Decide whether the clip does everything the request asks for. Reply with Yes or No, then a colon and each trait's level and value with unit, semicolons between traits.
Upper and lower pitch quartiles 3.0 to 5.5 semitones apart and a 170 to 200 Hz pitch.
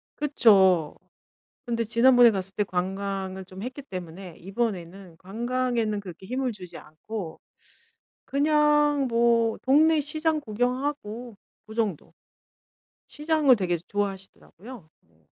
No: average, 5.2 semitones; high, 220 Hz